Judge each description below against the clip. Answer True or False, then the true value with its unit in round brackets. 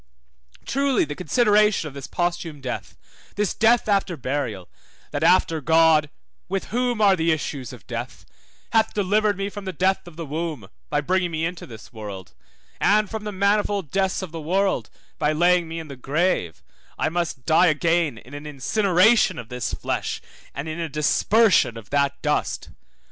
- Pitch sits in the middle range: True (165 Hz)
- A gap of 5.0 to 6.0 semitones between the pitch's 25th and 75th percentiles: True (5.6 semitones)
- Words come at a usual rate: True (175 wpm)